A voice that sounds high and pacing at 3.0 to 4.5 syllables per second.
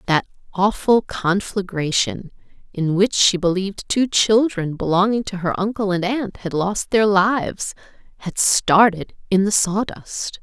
Yes: high, 195 Hz; 4.2 syllables/s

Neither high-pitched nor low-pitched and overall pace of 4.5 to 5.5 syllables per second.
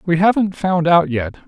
Yes: medium, 170 Hz; 4.8 syllables/s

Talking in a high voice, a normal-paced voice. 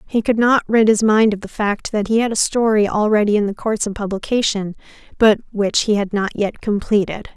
No: high, 210 Hz; fast, 220 wpm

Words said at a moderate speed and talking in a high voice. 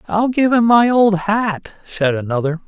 Yes: average, 180 wpm; high, 200 Hz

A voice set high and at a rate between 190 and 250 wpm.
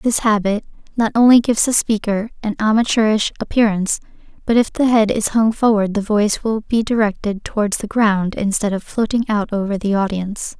No: high, 215 Hz; average, 180 wpm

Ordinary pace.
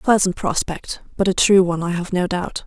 No: fast, 250 wpm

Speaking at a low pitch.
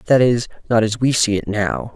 Yes: low, 110 Hz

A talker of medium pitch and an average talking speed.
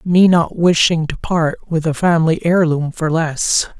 Yes: medium, 165 Hz; average, 175 wpm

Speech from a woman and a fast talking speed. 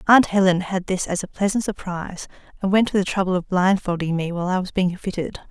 Yes: female; fast, 230 wpm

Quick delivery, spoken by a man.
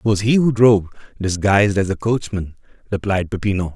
No: average, 175 wpm; male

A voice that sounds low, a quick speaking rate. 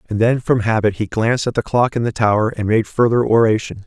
Yes: low, 110 Hz; fast, 250 wpm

